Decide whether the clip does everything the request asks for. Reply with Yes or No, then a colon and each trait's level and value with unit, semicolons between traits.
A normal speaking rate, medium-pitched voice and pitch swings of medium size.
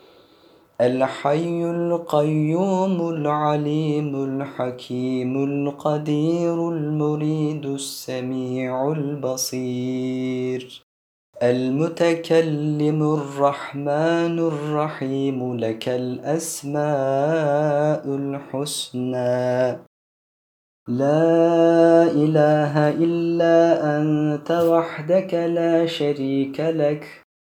No: slow, 50 wpm; medium, 150 Hz; average, 3.5 semitones